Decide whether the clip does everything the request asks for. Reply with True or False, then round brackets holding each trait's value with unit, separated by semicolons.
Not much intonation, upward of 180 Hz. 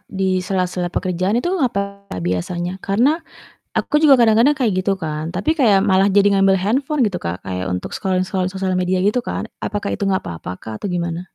False (3.0 semitones; 190 Hz)